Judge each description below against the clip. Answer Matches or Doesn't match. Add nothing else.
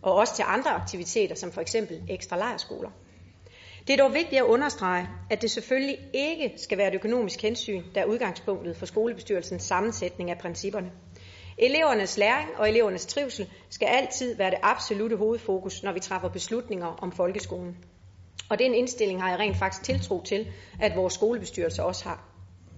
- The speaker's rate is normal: Matches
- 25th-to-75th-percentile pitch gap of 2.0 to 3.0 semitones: Doesn't match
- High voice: Matches